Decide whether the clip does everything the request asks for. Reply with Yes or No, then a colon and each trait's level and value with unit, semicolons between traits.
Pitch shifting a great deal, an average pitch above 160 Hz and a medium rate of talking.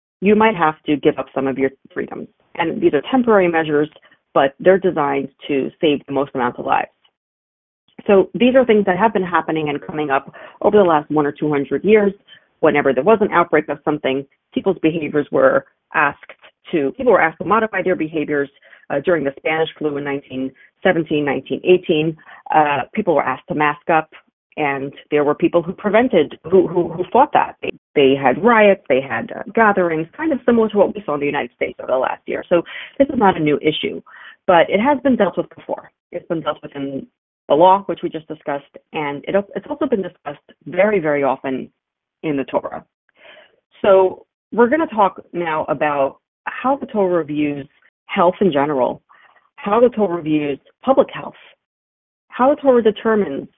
Yes: wide, 5.8 semitones; medium, 170 Hz; average, 195 wpm